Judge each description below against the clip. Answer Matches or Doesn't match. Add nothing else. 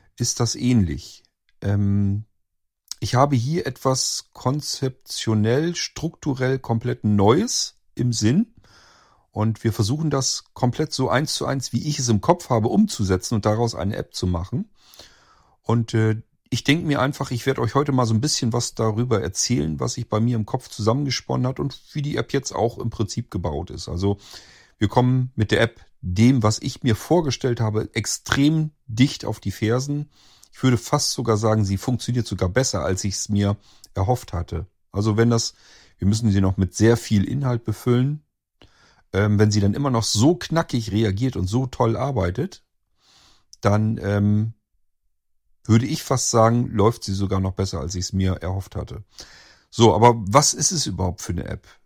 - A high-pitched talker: Doesn't match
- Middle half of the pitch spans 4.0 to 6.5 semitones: Matches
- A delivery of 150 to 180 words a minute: Matches